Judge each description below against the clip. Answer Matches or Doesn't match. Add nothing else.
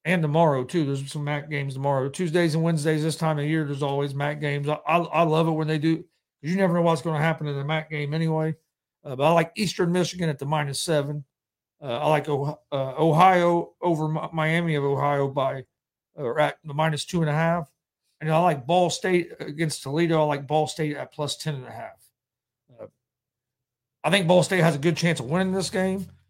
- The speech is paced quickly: Matches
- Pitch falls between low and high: Matches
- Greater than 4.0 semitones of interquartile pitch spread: Doesn't match